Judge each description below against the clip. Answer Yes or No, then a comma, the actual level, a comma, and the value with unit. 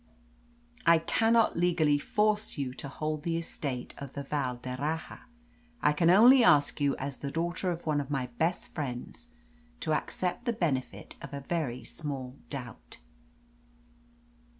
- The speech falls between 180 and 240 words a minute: No, average, 150 wpm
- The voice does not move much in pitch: No, average, 3.9 semitones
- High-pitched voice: No, medium, 150 Hz